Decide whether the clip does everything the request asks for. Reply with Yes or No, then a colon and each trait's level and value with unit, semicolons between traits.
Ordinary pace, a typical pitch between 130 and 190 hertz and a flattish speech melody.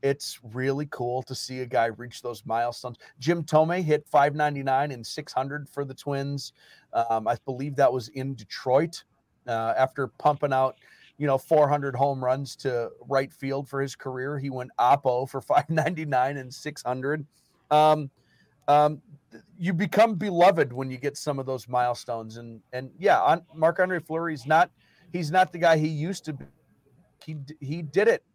No: average, 165 wpm; medium, 140 Hz; average, 3.1 semitones